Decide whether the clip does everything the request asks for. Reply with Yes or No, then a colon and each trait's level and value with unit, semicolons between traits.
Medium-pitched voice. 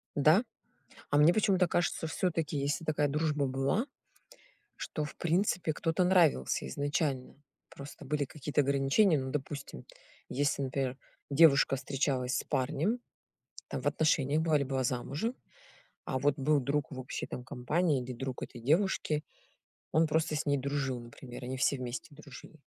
Yes: medium, 145 Hz